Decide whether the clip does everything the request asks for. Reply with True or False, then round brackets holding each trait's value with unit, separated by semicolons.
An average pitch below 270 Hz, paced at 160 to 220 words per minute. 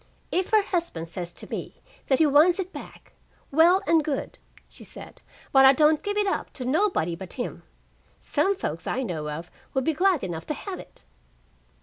False (300 Hz; 195 wpm)